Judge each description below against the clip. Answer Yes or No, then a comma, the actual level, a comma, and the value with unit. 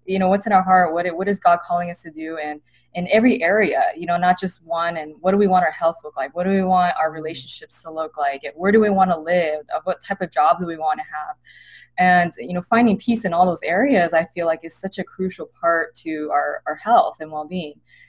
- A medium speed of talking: No, fast, 270 wpm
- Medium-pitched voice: Yes, medium, 175 Hz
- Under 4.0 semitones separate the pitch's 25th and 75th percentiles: Yes, average, 3.0 semitones